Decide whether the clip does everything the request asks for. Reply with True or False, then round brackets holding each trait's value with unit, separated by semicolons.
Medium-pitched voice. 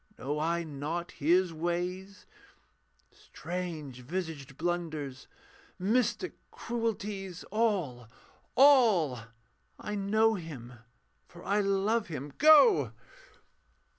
True (175 Hz)